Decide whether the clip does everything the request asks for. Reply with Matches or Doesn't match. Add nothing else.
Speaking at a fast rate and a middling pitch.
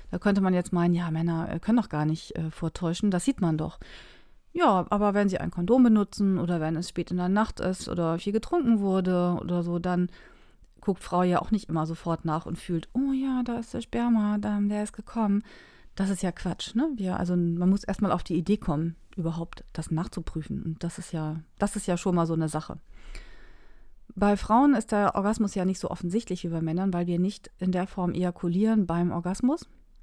Matches